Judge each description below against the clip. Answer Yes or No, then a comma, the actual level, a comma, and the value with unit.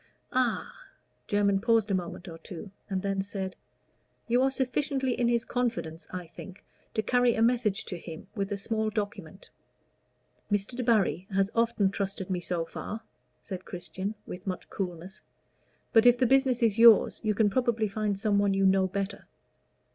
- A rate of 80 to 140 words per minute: No, average, 170 wpm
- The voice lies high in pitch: Yes, high, 205 Hz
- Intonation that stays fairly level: No, average, 3.5 semitones